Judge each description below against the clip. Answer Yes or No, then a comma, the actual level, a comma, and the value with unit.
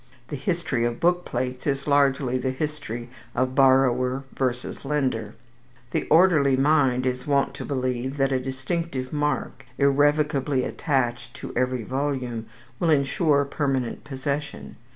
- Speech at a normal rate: No, slow, 130 wpm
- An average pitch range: No, narrow, 2.3 semitones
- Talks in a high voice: No, low, 135 Hz